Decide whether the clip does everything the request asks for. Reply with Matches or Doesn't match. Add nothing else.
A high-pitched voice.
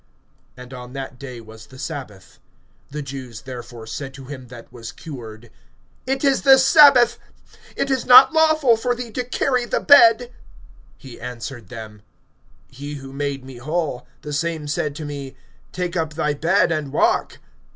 Doesn't match